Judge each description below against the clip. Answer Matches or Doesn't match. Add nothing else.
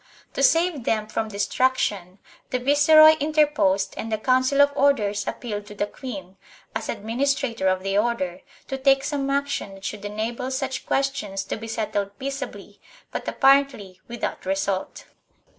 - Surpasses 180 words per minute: Doesn't match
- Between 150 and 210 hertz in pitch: Doesn't match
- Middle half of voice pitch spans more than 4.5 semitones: Matches